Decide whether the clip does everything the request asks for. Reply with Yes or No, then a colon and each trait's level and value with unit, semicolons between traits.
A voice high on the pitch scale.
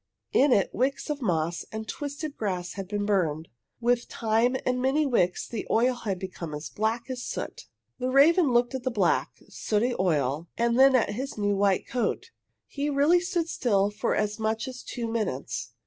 Yes: high, 230 Hz